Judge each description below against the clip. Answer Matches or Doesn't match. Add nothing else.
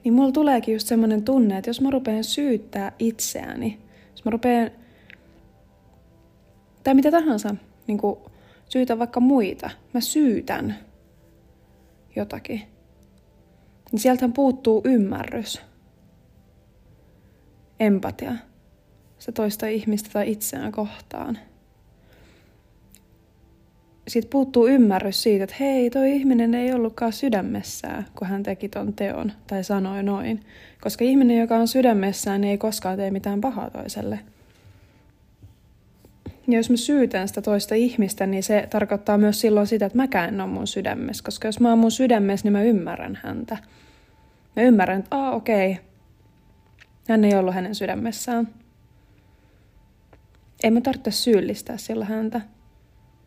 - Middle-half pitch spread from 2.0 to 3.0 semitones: Doesn't match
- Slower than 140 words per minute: Matches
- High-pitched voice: Matches